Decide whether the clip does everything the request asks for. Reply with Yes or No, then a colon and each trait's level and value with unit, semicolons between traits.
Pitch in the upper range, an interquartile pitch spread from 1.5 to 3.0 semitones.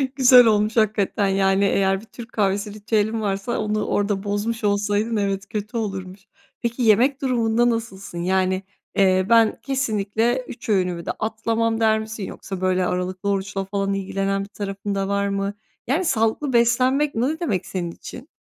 Yes: high, 205 Hz; narrow, 2.6 semitones